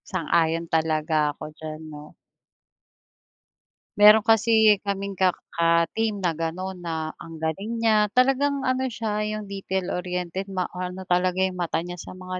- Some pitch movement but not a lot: Yes, average, 3.9 semitones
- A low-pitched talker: No, medium, 185 Hz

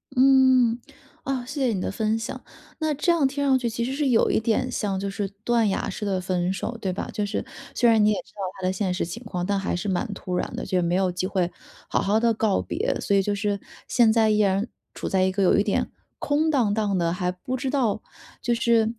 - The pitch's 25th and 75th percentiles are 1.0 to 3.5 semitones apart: No, average, 4.1 semitones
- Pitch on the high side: Yes, high, 215 Hz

